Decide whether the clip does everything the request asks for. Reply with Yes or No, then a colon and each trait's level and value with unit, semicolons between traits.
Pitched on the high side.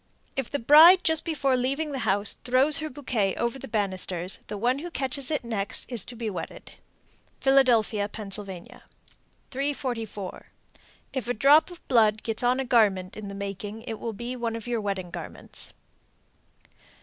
Yes: high, 235 Hz